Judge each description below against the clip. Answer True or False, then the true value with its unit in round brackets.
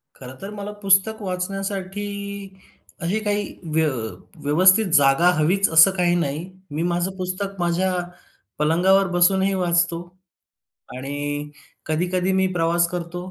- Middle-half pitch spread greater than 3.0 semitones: False (2.7 semitones)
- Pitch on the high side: False (180 Hz)